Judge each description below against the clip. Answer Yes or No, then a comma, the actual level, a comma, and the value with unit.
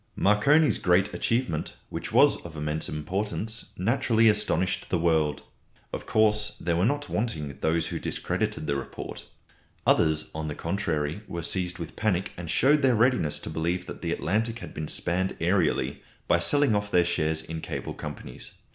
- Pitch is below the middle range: Yes, very low, 90 Hz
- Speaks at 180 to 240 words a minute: No, average, 165 wpm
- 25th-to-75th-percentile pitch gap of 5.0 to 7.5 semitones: Yes, average, 5.3 semitones